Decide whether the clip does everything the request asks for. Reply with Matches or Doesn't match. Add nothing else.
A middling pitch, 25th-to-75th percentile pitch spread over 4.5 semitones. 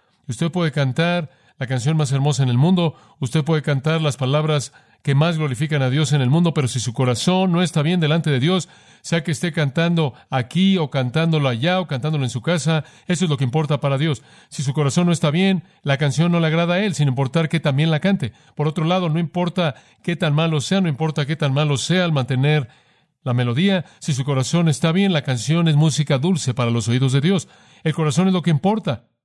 Doesn't match